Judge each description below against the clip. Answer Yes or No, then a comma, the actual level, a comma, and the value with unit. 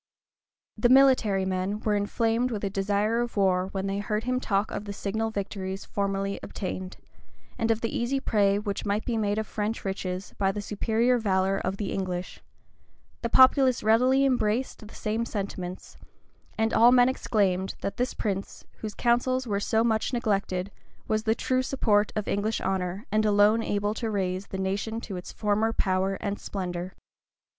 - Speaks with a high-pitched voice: Yes, high, 210 Hz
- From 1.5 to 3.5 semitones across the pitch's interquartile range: Yes, narrow, 2.6 semitones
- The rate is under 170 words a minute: No, average, 175 wpm